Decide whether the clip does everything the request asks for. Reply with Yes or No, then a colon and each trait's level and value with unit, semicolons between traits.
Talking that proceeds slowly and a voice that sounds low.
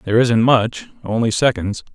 Yes: slow, 125 wpm; low, 120 Hz